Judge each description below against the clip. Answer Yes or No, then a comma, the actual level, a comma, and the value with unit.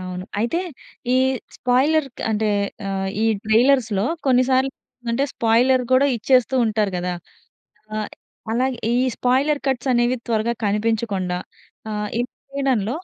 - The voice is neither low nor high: No, high, 235 Hz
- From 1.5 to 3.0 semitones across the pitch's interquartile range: No, average, 3.6 semitones